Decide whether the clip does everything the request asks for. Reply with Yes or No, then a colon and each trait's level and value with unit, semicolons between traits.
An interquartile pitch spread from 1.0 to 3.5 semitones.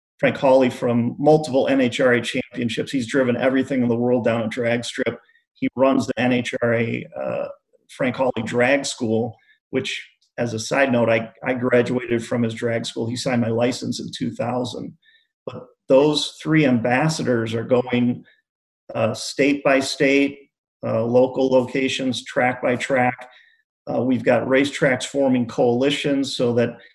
Yes: average, 2.7 semitones